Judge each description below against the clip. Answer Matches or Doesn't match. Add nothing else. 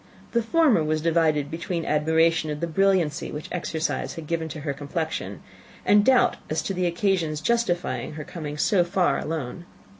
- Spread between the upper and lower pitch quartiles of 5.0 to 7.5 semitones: Doesn't match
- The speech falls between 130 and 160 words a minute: Doesn't match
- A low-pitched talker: Doesn't match